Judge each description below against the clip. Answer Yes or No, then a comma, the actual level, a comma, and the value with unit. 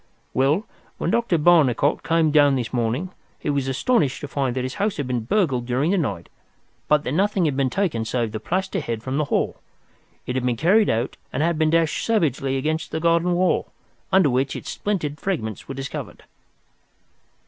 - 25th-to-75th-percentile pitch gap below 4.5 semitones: No, average, 5.0 semitones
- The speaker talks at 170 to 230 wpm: Yes, average, 190 wpm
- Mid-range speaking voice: Yes, medium, 145 Hz